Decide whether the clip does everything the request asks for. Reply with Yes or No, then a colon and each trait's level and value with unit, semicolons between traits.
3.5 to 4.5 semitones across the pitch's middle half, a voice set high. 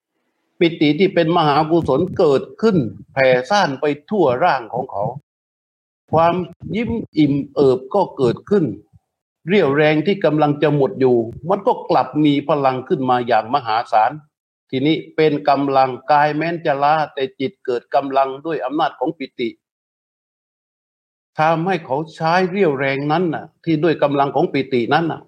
No: average, 3.8 semitones; medium, 150 Hz